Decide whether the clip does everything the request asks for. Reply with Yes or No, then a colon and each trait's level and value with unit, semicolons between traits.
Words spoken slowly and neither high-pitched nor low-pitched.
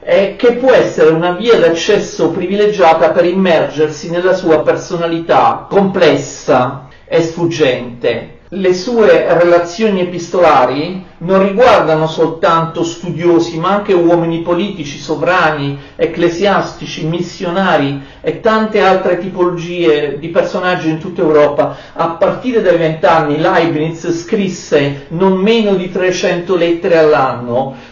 Yes: slow, 110 wpm; medium, 170 Hz